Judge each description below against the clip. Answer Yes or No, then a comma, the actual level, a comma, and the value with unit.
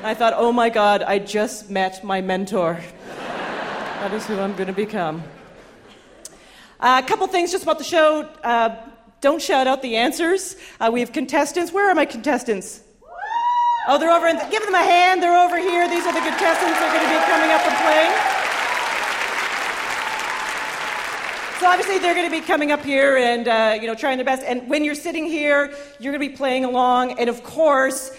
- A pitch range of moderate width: No, wide, 6.9 semitones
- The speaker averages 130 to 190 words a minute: No, average, 200 wpm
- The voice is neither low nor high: No, very high, 275 Hz